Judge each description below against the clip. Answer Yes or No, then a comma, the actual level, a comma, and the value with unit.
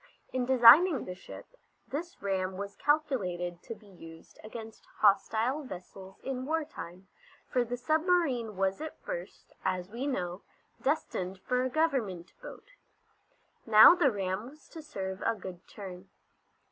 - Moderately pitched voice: No, high, 220 Hz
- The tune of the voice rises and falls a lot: Yes, wide, 6.7 semitones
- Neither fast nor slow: Yes, average, 145 wpm